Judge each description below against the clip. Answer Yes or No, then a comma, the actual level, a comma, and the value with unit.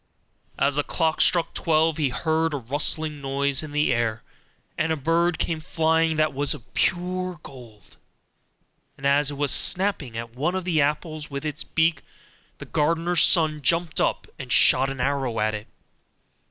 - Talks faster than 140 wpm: Yes, average, 170 wpm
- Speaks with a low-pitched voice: No, medium, 150 Hz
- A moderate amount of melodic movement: Yes, average, 3.1 semitones